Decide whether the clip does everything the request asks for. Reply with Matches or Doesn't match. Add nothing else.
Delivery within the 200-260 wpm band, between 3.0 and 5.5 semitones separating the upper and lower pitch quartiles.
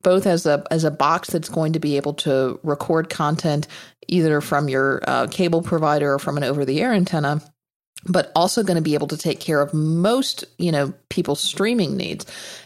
Matches